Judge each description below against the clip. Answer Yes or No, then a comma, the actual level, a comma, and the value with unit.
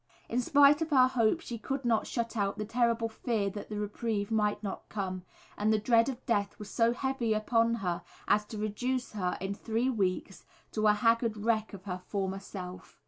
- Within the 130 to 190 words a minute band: No, average, 200 wpm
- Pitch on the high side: Yes, high, 220 Hz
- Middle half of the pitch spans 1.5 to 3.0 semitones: Yes, narrow, 2.6 semitones